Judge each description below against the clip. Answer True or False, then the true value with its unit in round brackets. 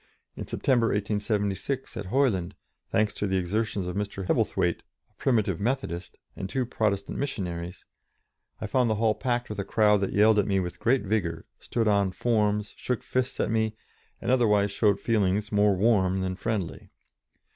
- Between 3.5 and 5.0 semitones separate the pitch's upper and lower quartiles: False (2.8 semitones)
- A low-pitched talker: True (105 Hz)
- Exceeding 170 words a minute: False (165 wpm)